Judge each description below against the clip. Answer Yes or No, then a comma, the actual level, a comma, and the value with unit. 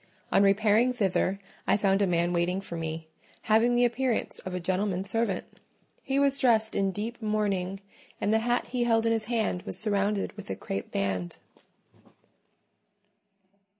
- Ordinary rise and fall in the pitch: Yes, average, 3.6 semitones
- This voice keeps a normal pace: Yes, average, 160 wpm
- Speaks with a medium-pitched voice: No, high, 205 Hz